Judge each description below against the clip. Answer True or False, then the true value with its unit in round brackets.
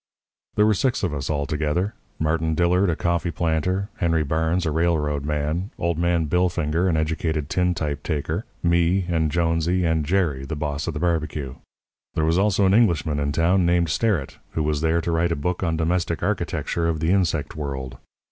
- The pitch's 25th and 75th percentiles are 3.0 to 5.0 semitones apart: False (2.5 semitones)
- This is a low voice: True (80 Hz)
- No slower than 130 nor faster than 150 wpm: False (185 wpm)